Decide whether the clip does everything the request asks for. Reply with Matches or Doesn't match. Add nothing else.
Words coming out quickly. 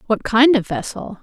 Doesn't match